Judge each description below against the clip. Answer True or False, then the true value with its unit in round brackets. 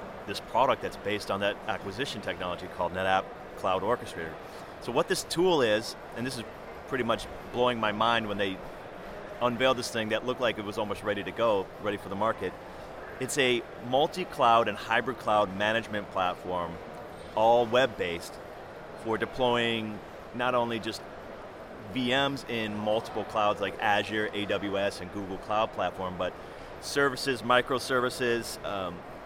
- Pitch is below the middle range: True (110 Hz)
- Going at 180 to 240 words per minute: False (155 wpm)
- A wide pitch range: False (3.5 semitones)